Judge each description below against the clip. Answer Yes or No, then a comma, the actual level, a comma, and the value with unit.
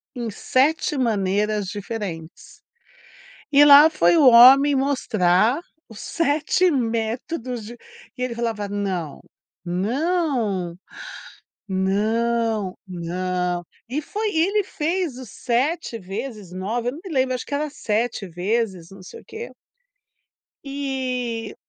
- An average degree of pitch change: No, wide, 6.0 semitones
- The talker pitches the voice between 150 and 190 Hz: No, high, 235 Hz